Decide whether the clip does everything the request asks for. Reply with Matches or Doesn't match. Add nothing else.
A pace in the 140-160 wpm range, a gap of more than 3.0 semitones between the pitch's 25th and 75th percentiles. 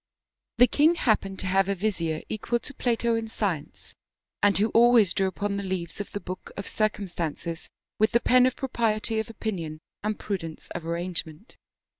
Doesn't match